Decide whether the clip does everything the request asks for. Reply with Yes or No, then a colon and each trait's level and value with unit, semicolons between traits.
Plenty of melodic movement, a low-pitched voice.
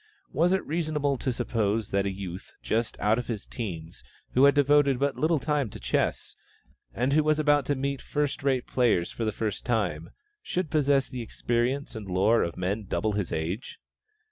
Yes: wide, 5.7 semitones; low, 125 Hz